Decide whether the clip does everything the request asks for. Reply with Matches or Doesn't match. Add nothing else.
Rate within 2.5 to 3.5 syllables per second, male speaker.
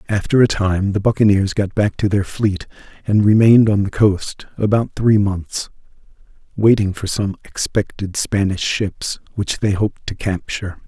Doesn't match